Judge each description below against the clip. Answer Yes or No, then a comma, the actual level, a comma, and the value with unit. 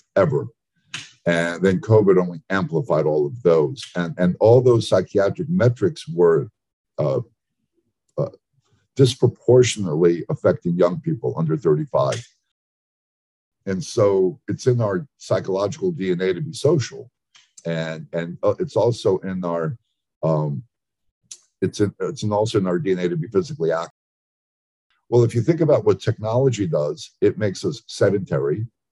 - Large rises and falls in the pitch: Yes, wide, 6.6 semitones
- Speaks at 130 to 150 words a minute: Yes, slow, 135 wpm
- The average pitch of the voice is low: Yes, low, 100 Hz